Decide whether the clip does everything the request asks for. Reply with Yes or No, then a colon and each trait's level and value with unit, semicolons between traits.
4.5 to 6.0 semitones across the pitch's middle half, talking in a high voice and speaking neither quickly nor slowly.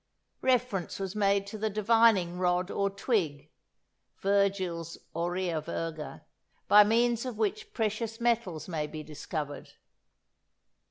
No: average, 4.9 semitones; high, 195 Hz; slow, 115 wpm